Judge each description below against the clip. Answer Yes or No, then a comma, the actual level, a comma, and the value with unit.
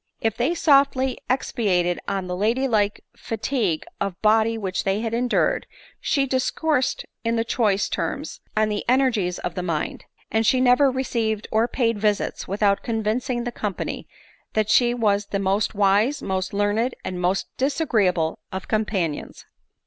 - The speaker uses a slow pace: No, average, 155 wpm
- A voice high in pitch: Yes, high, 220 Hz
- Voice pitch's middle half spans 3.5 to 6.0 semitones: Yes, average, 3.8 semitones